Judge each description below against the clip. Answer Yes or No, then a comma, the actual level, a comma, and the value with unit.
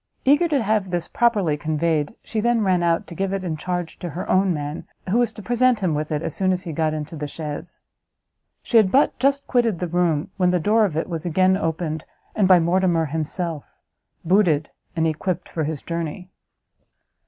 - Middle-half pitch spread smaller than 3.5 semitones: No, average, 3.8 semitones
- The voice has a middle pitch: Yes, medium, 175 Hz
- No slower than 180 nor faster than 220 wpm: Yes, average, 200 wpm